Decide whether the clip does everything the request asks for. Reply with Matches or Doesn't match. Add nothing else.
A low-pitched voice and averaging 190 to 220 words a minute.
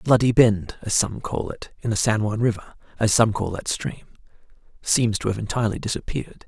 Matches